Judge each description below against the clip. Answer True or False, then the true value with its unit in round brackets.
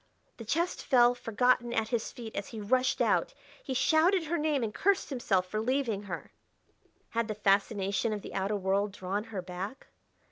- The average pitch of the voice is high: True (225 Hz)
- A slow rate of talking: False (180 wpm)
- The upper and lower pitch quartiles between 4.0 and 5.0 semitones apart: True (4.3 semitones)